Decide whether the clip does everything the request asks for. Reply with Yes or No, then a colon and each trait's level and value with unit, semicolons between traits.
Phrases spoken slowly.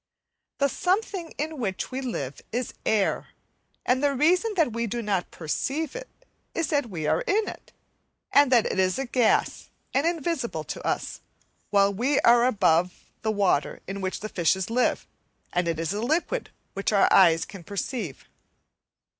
No: average, 170 wpm